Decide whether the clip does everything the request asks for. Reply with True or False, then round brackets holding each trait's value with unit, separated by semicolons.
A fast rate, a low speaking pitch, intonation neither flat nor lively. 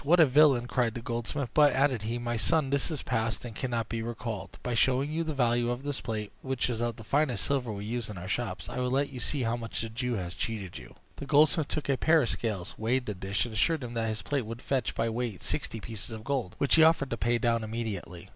True (260 wpm; 120 Hz; 3.4 semitones)